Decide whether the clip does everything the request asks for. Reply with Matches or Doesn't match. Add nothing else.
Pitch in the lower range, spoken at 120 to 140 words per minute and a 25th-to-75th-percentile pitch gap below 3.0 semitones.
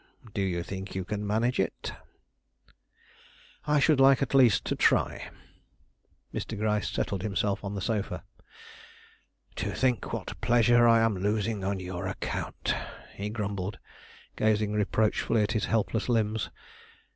Matches